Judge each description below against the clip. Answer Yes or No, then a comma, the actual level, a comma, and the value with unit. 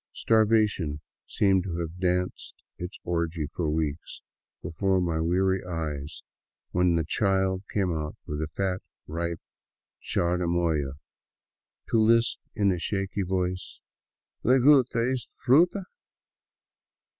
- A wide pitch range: No, average, 3.3 semitones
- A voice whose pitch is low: Yes, very low, 90 Hz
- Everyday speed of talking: No, slow, 120 wpm